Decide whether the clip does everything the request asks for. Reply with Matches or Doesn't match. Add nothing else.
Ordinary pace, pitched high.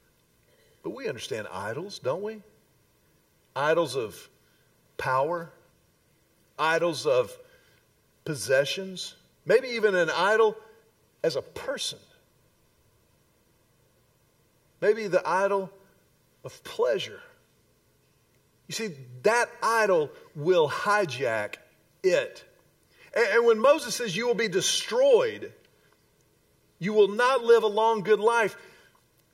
Doesn't match